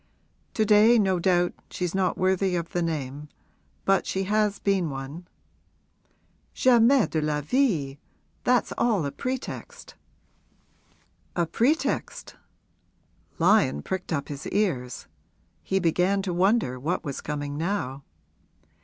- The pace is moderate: No, slow, 120 wpm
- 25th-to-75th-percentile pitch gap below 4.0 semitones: No, wide, 5.5 semitones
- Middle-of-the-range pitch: Yes, medium, 180 Hz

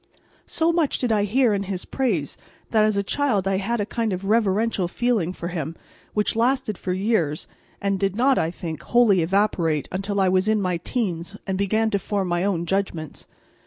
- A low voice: No, high, 200 Hz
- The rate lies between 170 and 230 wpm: Yes, average, 200 wpm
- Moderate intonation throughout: Yes, average, 3.4 semitones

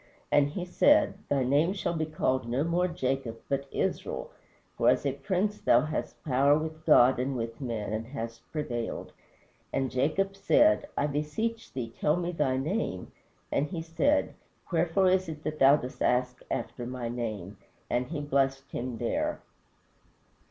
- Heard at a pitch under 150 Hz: Yes, medium, 140 Hz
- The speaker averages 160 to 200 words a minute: Yes, average, 165 wpm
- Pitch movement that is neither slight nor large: Yes, average, 4.8 semitones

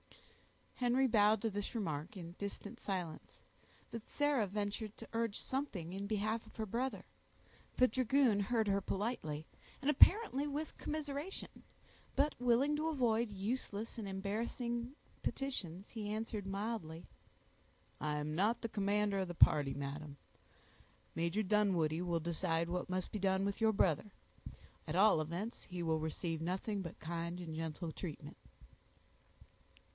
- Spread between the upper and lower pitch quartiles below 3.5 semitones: No, average, 5.3 semitones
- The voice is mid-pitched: No, high, 205 Hz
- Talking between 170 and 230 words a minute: No, average, 140 wpm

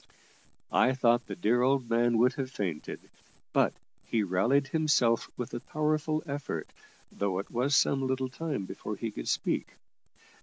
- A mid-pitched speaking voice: No, low, 125 Hz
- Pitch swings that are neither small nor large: Yes, average, 3.6 semitones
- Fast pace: No, average, 155 wpm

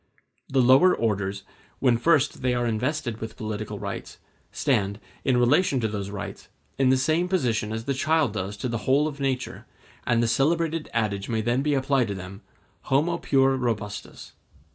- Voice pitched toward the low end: Yes, low, 125 Hz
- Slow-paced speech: No, average, 175 wpm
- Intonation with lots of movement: No, average, 4.4 semitones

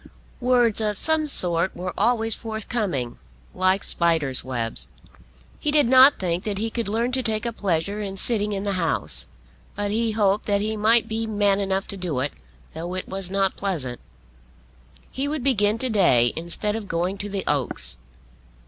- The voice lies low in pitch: No, high, 200 Hz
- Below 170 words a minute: No, average, 175 wpm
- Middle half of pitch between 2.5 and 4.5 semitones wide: Yes, average, 4.1 semitones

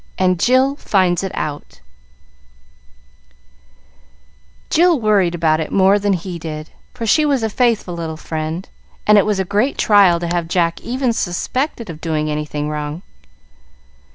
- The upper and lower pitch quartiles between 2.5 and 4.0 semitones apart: No, average, 5.3 semitones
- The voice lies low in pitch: No, medium, 185 Hz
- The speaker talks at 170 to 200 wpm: No, average, 150 wpm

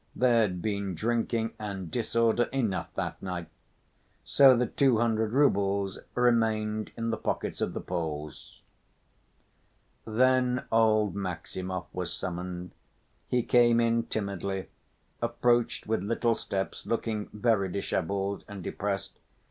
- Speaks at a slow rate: Yes, slow, 120 wpm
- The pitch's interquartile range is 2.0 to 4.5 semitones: Yes, average, 3.3 semitones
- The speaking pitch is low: Yes, low, 110 Hz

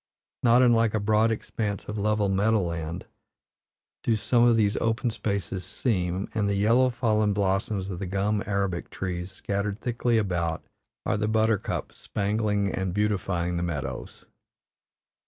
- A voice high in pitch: No, low, 105 Hz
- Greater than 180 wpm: No, average, 145 wpm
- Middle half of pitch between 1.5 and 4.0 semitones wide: Yes, average, 2.7 semitones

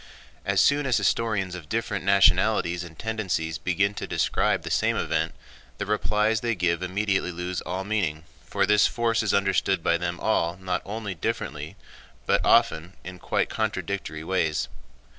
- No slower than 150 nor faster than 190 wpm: Yes, average, 160 wpm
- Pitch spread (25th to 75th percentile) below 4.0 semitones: Yes, average, 3.5 semitones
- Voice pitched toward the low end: Yes, very low, 95 Hz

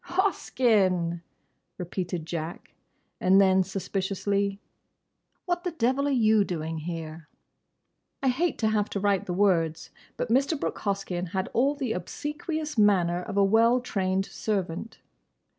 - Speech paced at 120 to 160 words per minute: Yes, average, 140 wpm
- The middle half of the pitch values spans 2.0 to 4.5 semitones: No, wide, 5.4 semitones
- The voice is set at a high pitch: Yes, high, 200 Hz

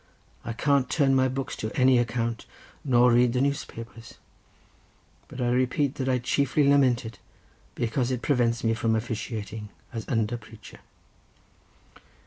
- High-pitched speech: No, low, 120 Hz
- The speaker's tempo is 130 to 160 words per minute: Yes, average, 140 wpm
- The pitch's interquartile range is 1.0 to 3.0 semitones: Yes, narrow, 2.4 semitones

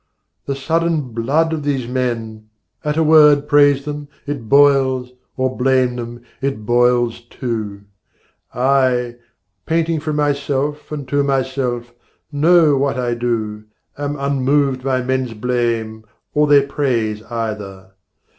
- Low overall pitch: Yes, low, 130 Hz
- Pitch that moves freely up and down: No, average, 3.2 semitones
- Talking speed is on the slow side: Yes, slow, 125 wpm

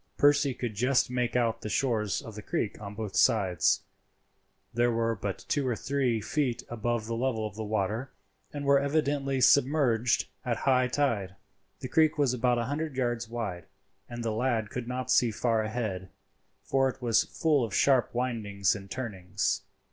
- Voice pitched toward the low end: Yes, low, 120 Hz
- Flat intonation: No, average, 3.4 semitones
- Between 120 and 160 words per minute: No, average, 175 wpm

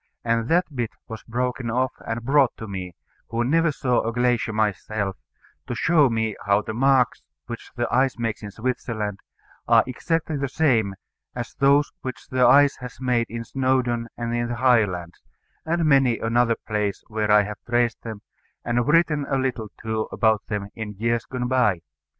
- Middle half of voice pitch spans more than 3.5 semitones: No, average, 2.9 semitones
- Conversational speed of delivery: Yes, average, 175 wpm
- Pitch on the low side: Yes, low, 120 Hz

